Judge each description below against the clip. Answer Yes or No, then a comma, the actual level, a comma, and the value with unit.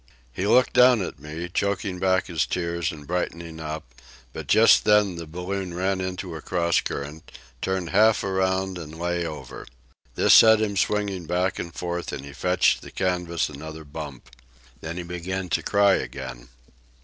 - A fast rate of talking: No, average, 170 wpm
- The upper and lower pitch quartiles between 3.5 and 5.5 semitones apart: No, average, 2.9 semitones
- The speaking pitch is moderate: No, very low, 90 Hz